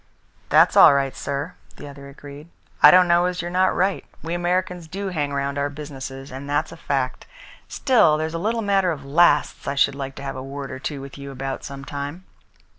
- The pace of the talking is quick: Yes, fast, 215 wpm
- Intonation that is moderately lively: Yes, average, 4.0 semitones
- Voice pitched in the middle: Yes, medium, 145 Hz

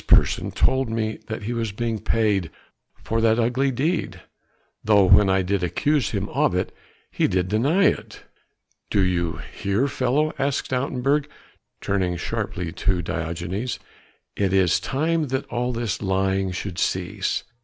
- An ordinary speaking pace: Yes, average, 150 wpm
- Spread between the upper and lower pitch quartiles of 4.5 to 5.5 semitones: Yes, average, 5.2 semitones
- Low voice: Yes, low, 110 Hz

